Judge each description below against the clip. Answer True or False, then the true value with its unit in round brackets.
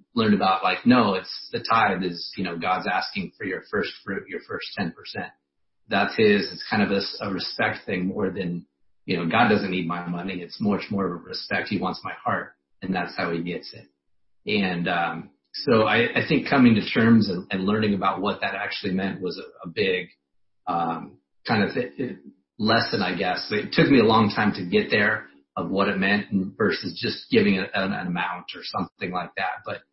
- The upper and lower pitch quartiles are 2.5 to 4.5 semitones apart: True (2.8 semitones)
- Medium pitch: False (95 Hz)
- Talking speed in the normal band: False (215 wpm)